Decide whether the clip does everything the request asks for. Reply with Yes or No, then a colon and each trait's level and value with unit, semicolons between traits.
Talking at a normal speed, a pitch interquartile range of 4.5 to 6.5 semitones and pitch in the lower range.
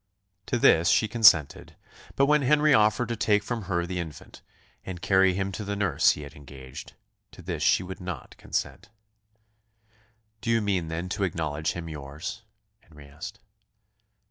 Yes: average, 165 wpm; average, 5.2 semitones; very low, 95 Hz